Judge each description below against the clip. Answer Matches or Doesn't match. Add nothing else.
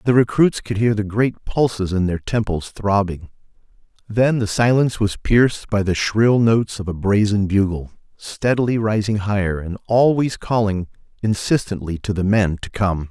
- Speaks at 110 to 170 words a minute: Matches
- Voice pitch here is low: Matches